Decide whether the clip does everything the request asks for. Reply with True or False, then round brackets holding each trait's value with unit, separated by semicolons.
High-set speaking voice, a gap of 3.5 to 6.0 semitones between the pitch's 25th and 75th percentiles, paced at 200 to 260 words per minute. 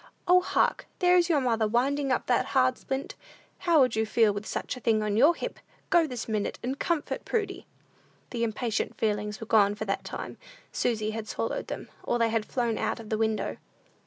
True (230 Hz; 4.3 semitones; 205 wpm)